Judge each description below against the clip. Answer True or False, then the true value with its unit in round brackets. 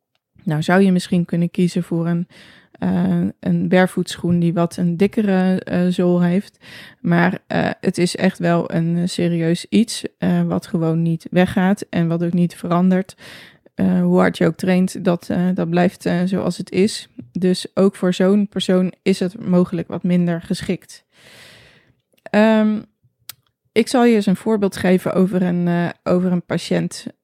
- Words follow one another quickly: False (165 wpm)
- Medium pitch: True (180 Hz)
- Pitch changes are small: True (1.6 semitones)